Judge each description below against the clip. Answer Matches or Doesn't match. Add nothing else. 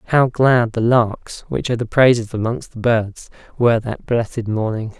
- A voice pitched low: Matches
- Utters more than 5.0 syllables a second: Doesn't match